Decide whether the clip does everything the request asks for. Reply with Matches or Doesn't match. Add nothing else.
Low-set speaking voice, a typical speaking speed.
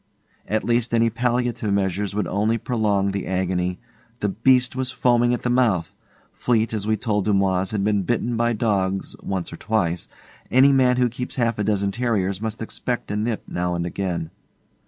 Matches